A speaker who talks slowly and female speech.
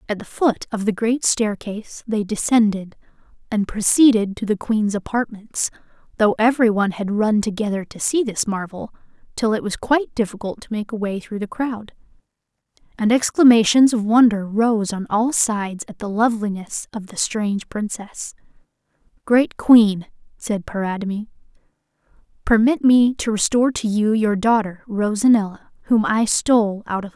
No: average, 155 wpm; female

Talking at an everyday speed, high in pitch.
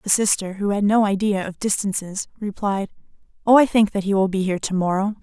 No: fast, 220 wpm; high, 200 Hz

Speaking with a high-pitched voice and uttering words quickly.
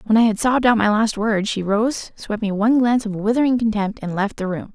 Yes: high, 220 Hz; fast, 265 wpm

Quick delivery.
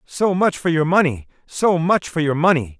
Yes: fast, 215 wpm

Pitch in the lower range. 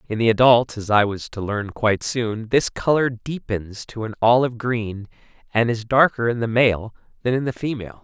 Yes: low, 115 Hz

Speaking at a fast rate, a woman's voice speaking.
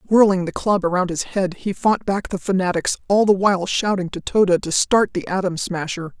Yes: fast, 215 wpm; female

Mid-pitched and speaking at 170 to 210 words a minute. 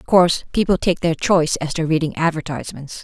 Yes: medium, 165 Hz; average, 200 wpm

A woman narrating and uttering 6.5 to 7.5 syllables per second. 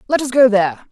Yes: female; 6.9 syllables/s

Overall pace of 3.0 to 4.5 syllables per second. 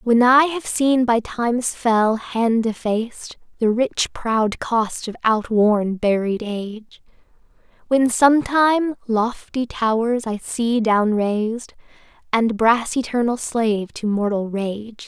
Yes: 3.6 syllables/s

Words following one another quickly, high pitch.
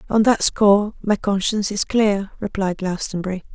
No: average, 150 wpm; high, 200 Hz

